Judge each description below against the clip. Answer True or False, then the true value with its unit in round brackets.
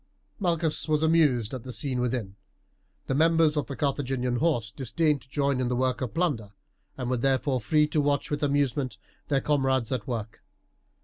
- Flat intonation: False (3.2 semitones)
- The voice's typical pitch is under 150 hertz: True (135 Hz)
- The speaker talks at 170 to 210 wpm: True (180 wpm)